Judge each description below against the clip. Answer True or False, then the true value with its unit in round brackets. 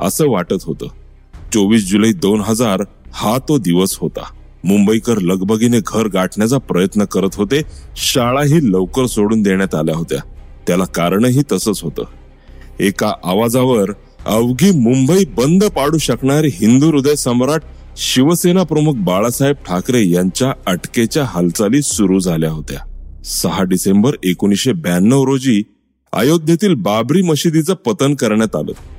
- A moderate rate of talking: True (120 wpm)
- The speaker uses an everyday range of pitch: False (7.2 semitones)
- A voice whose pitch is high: False (110 Hz)